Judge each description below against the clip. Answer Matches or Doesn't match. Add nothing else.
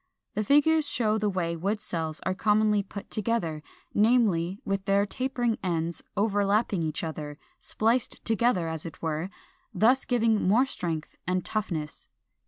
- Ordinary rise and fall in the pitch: Matches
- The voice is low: Doesn't match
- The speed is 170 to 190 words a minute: Doesn't match